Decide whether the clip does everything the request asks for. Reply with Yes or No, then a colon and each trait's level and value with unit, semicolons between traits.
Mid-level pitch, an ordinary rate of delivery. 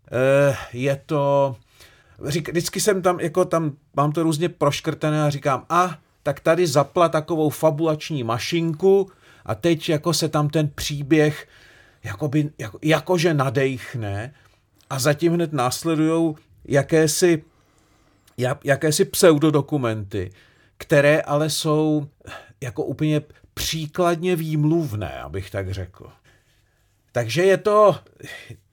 No: medium, 150 Hz; slow, 110 wpm